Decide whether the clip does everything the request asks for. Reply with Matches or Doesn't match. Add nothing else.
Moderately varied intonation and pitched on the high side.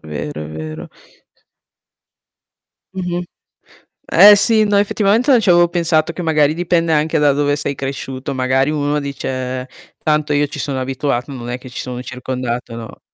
Doesn't match